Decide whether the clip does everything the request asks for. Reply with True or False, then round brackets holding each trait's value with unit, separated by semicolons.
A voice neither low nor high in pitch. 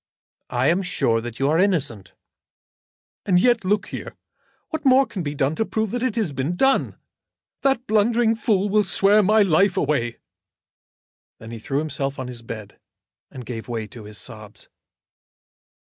True (170 Hz)